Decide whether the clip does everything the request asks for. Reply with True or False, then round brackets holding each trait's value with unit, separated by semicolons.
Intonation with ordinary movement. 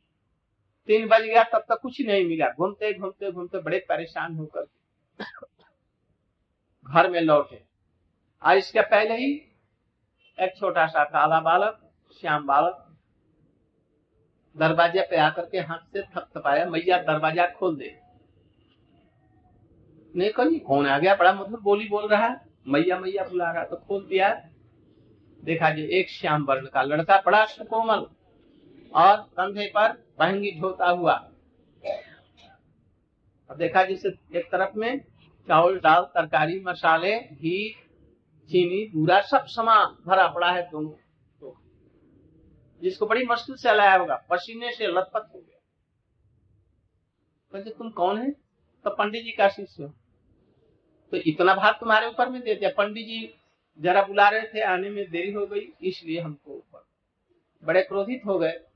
True (4.9 semitones)